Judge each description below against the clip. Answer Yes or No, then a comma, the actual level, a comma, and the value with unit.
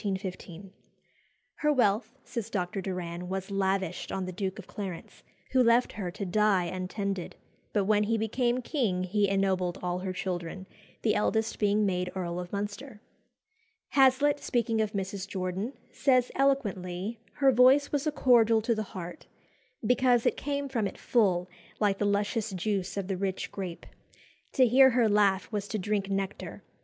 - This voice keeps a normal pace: Yes, average, 160 wpm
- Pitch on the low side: No, high, 205 Hz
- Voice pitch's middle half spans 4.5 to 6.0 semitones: No, average, 3.9 semitones